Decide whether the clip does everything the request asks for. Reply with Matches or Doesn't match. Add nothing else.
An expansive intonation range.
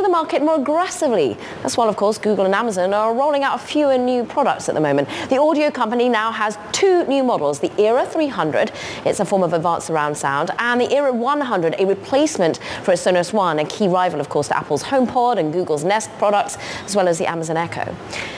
Matches